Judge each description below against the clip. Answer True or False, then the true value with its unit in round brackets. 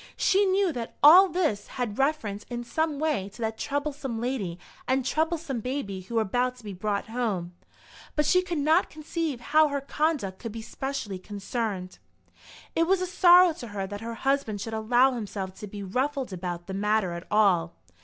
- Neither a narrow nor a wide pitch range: False (6.6 semitones)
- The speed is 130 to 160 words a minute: False (185 wpm)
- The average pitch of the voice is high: True (240 Hz)